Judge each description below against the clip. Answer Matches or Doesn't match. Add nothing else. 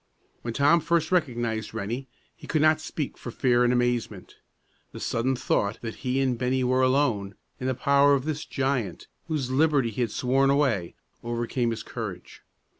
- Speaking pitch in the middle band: Doesn't match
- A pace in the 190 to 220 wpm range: Doesn't match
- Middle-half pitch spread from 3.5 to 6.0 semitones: Doesn't match